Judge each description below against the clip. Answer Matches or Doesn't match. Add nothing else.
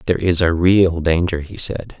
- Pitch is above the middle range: Doesn't match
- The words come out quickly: Matches